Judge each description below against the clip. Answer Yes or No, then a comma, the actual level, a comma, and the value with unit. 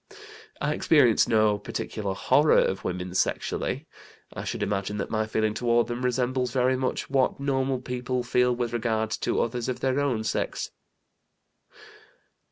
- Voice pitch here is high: No, low, 120 Hz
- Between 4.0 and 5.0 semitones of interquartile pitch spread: No, average, 2.8 semitones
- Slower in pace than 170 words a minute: Yes, average, 150 wpm